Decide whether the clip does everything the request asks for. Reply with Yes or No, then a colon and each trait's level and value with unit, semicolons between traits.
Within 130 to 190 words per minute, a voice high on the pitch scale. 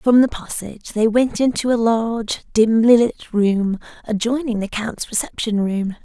Yes: average, 160 wpm; high, 225 Hz